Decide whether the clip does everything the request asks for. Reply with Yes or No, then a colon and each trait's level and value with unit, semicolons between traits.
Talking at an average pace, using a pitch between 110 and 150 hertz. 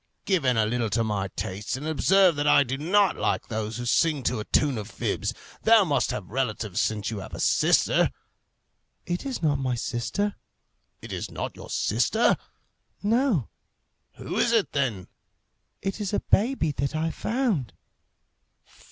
Yes: average, 170 wpm; medium, 140 Hz